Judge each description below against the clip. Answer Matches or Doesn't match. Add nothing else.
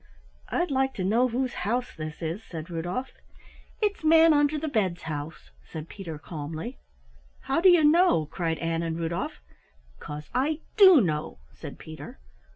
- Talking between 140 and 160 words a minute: Matches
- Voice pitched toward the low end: Doesn't match